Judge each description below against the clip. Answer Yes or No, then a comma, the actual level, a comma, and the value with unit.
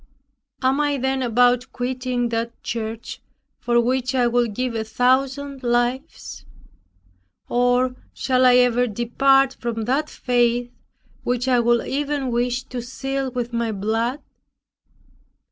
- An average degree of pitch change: No, narrow, 1.7 semitones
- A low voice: No, high, 245 Hz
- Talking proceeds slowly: Yes, slow, 130 wpm